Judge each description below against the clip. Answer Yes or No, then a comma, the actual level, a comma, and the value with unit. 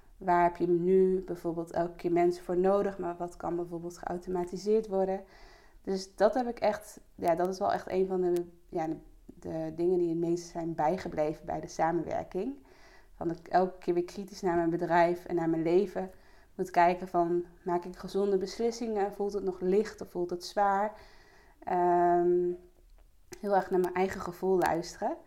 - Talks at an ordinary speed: Yes, average, 185 wpm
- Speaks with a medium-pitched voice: Yes, medium, 180 Hz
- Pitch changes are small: Yes, narrow, 1.8 semitones